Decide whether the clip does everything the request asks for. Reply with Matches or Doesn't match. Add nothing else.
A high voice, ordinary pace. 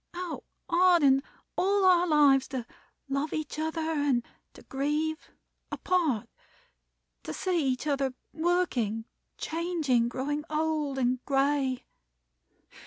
Doesn't match